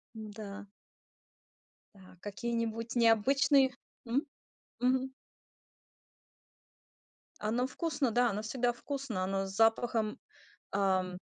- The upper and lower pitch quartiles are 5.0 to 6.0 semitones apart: No, average, 3.6 semitones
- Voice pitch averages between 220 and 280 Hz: Yes, high, 230 Hz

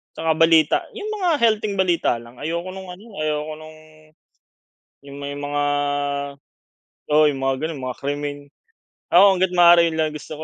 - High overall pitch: No, medium, 155 Hz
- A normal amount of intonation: Yes, average, 3.8 semitones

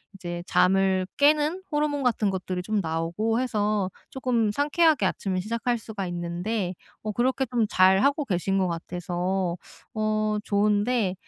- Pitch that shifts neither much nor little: Yes, average, 4.6 semitones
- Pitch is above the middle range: Yes, high, 210 Hz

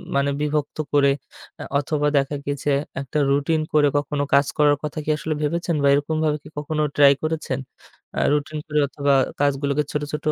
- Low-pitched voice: No, medium, 145 Hz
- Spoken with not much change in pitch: Yes, narrow, 1.2 semitones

